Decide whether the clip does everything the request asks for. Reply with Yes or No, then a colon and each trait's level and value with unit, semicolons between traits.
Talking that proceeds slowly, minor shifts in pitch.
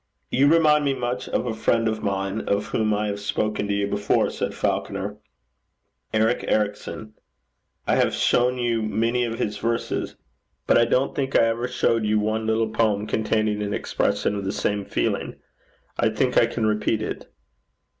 No: average, 175 wpm; narrow, 2.1 semitones